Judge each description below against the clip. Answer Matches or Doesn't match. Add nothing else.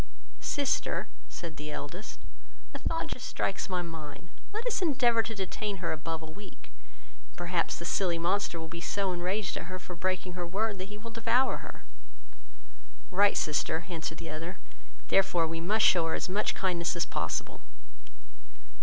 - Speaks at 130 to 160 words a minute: Doesn't match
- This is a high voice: Doesn't match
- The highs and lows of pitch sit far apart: Doesn't match